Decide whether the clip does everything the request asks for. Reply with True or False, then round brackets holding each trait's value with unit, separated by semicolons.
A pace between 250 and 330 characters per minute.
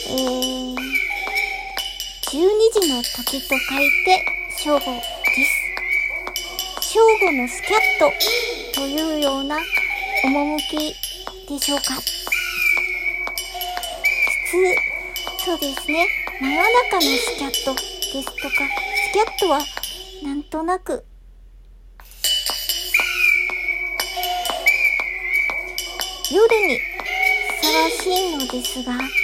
False (150 characters per minute)